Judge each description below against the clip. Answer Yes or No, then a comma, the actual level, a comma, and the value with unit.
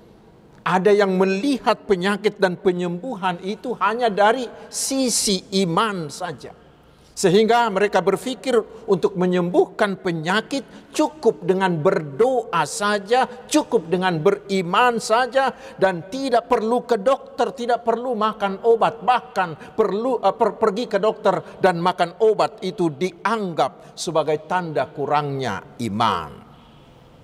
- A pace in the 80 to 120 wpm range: Yes, average, 110 wpm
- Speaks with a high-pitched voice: Yes, high, 210 Hz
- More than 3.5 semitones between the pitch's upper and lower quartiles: Yes, average, 4.0 semitones